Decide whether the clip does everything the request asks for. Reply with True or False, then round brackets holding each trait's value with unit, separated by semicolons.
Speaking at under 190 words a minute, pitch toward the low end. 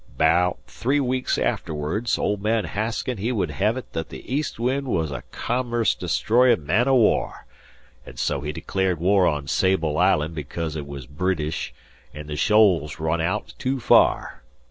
True (165 wpm; 95 Hz)